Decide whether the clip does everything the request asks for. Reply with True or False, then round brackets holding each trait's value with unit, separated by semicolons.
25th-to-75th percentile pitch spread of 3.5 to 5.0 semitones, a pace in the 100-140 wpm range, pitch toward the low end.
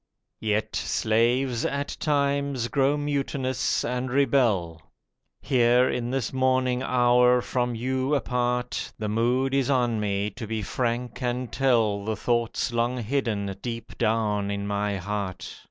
False (3.0 semitones; 135 wpm; 120 Hz)